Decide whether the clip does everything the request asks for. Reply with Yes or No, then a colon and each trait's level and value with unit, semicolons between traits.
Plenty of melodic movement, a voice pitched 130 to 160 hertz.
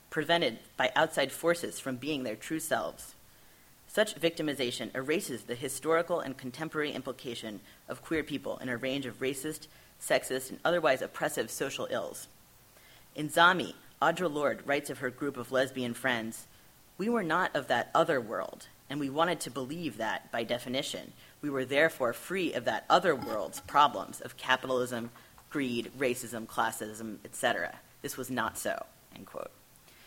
No: average, 4.2 semitones; low, 135 Hz